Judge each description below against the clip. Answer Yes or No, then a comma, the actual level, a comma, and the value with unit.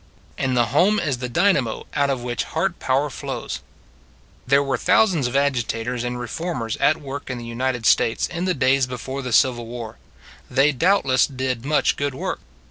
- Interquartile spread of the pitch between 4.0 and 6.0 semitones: No, average, 2.7 semitones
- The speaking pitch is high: No, low, 130 Hz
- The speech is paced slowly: No, average, 180 wpm